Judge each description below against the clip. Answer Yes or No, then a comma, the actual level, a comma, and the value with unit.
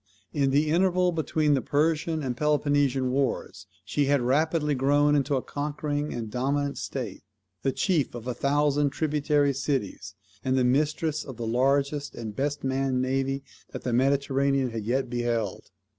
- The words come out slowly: No, average, 160 wpm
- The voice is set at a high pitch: No, medium, 140 Hz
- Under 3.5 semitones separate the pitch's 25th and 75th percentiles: Yes, narrow, 2.4 semitones